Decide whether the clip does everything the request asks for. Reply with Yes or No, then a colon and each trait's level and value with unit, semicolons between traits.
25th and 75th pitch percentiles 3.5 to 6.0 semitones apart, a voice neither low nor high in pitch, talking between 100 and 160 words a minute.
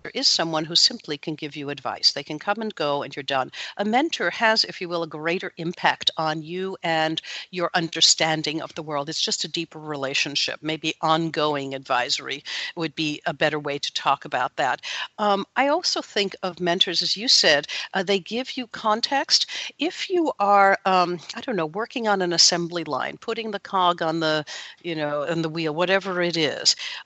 No: average, 4.5 semitones; medium, 170 Hz; average, 200 wpm